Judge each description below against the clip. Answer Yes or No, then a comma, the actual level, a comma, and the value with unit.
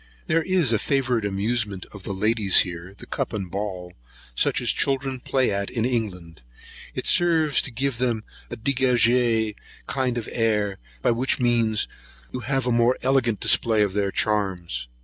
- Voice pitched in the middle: No, low, 115 Hz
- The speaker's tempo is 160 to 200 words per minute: Yes, average, 170 wpm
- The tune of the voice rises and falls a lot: No, average, 4.0 semitones